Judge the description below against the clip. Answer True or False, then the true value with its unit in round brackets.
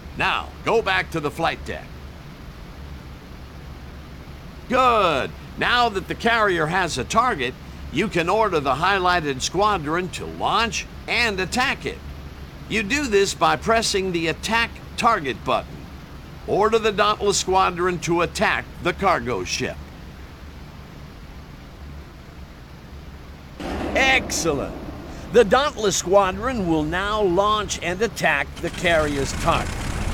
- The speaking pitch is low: False (170 Hz)